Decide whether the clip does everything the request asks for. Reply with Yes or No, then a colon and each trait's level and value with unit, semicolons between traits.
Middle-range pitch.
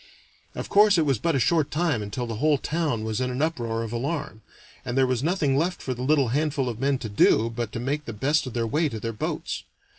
No: low, 130 Hz